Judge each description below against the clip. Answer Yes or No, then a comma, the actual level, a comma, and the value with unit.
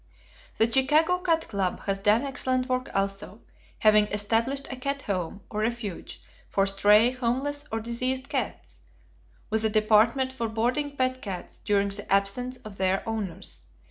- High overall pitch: Yes, high, 225 Hz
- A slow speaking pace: No, average, 150 wpm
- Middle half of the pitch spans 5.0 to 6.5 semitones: No, average, 4.2 semitones